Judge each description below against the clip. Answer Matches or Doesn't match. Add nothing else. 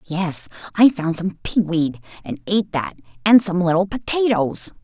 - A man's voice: Doesn't match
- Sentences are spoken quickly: Doesn't match